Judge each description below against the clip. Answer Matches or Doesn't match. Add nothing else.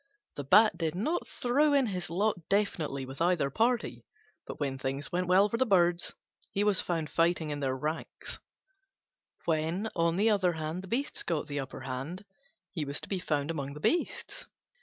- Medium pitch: Matches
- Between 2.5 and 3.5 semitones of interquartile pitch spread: Doesn't match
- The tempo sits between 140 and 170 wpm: Doesn't match